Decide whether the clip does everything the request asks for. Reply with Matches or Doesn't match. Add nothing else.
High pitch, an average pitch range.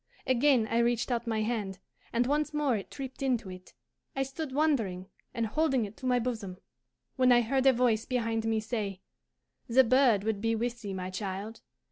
Matches